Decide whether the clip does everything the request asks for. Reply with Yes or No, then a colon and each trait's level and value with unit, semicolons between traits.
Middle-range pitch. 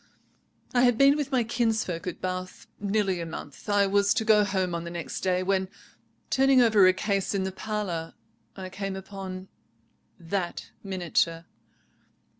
No: high, 195 Hz